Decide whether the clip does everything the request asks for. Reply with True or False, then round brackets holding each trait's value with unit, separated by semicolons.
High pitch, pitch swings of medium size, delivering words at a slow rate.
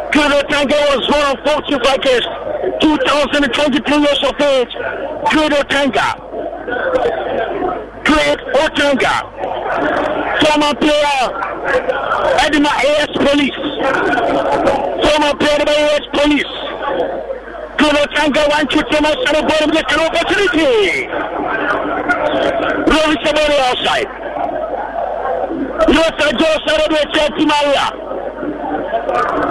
False (295 Hz; 1.2 semitones; 70 wpm)